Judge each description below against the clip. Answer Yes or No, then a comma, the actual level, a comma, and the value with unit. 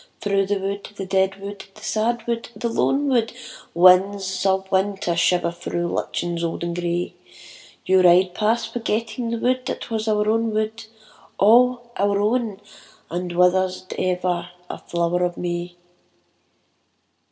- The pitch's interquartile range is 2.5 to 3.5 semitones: No, average, 3.9 semitones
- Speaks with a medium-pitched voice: No, high, 195 Hz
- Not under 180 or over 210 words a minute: No, average, 150 wpm